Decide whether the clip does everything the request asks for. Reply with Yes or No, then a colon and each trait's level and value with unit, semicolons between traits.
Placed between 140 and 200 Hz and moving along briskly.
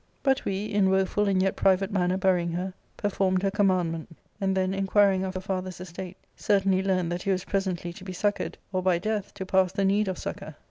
Yes: high, 190 Hz; fast, 225 wpm